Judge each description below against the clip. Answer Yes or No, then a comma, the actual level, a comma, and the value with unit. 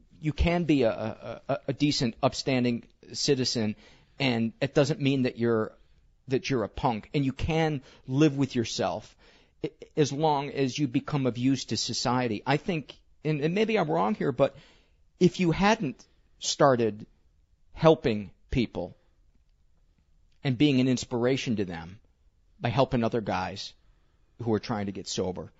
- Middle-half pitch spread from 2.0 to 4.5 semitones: No, wide, 5.4 semitones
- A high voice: No, low, 125 Hz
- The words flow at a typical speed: Yes, average, 150 wpm